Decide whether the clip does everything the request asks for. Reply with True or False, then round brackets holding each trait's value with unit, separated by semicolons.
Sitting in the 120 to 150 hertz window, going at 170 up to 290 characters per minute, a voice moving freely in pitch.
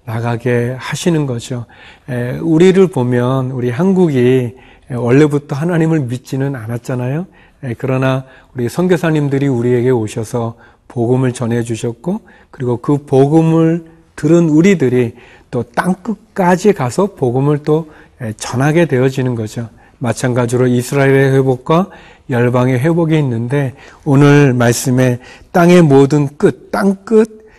False (135 Hz; 280 characters per minute; 4.8 semitones)